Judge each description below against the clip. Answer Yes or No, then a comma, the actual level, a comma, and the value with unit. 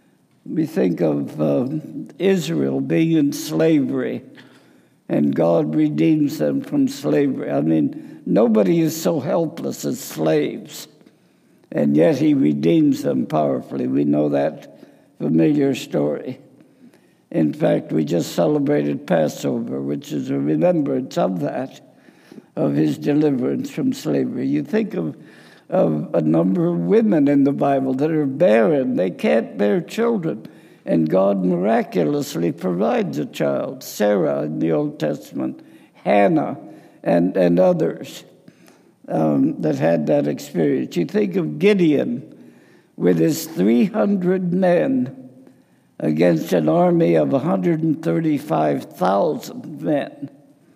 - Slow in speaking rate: Yes, slow, 120 wpm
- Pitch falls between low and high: Yes, medium, 150 Hz